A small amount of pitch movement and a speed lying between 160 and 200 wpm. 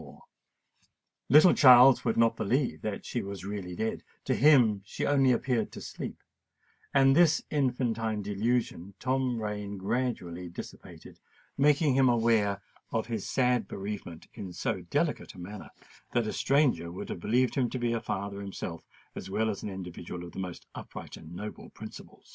No: average, 4.4 semitones; average, 165 wpm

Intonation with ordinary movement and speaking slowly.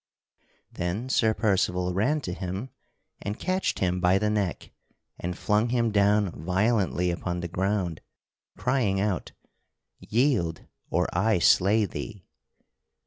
Yes: average, 3.4 semitones; slow, 125 wpm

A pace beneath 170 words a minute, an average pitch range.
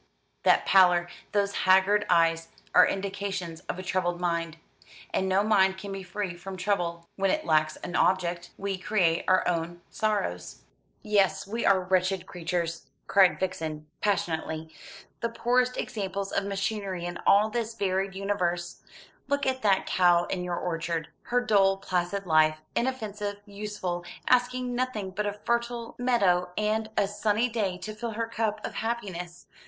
Yes: average, 155 wpm; average, 3.3 semitones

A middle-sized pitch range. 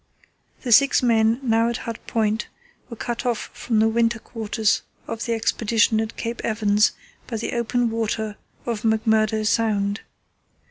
No: narrow, 1.2 semitones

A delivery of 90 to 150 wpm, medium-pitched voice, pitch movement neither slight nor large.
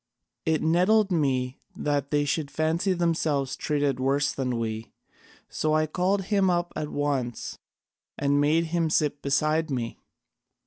Yes: average, 140 wpm; medium, 150 Hz; average, 3.1 semitones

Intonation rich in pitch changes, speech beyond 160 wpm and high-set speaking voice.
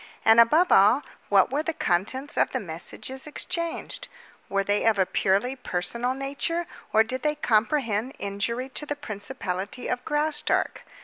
No: wide, 6.0 semitones; average, 150 wpm; very high, 250 Hz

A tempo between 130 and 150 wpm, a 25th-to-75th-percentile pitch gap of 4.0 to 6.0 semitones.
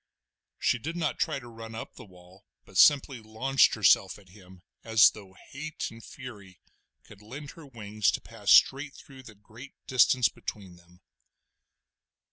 No: average, 160 wpm; average, 5.0 semitones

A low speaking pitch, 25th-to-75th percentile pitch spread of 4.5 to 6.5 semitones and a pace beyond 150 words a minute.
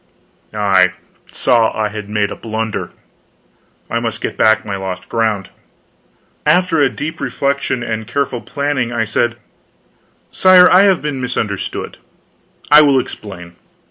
No: low, 115 Hz; average, 5.1 semitones; slow, 135 wpm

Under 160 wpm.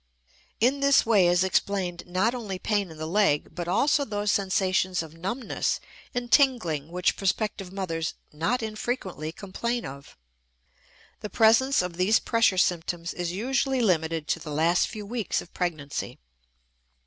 Yes: average, 150 wpm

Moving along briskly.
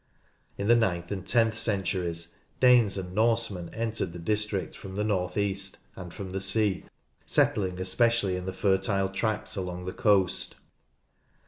No: average, 150 wpm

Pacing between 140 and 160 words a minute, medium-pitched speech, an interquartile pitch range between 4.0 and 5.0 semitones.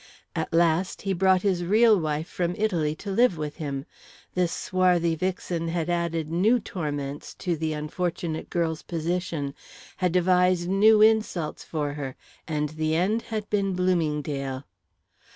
No: average, 145 wpm; medium, 170 Hz; average, 3.0 semitones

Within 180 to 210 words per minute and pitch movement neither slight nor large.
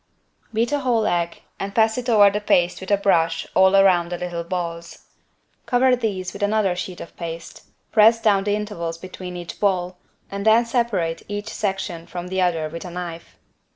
Yes: average, 190 wpm; average, 3.4 semitones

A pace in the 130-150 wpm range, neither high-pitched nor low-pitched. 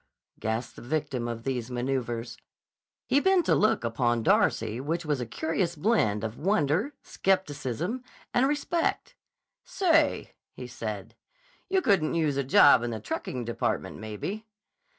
Yes: average, 140 wpm; medium, 145 Hz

